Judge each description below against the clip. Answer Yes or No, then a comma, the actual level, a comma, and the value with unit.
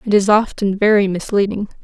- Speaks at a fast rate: No, average, 165 wpm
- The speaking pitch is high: Yes, high, 200 Hz